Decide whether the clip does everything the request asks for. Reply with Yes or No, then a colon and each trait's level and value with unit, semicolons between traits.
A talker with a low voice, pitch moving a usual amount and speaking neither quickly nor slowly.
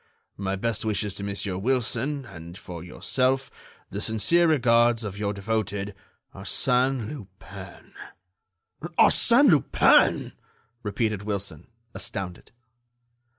No: low, 105 Hz; average, 3.7 semitones; slow, 100 wpm